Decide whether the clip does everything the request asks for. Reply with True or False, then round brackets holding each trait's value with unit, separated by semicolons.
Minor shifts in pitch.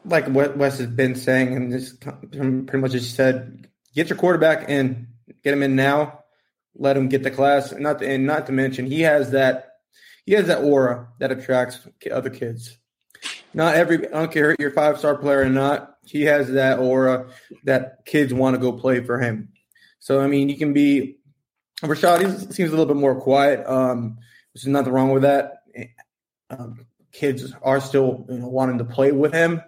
True (2.2 semitones)